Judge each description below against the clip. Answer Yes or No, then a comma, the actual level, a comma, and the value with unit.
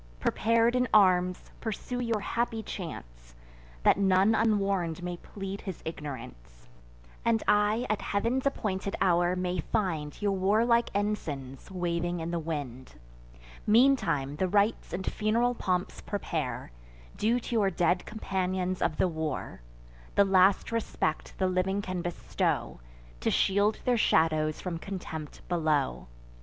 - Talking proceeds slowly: Yes, slow, 130 wpm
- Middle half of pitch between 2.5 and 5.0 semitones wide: Yes, average, 4.3 semitones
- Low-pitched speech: No, medium, 185 Hz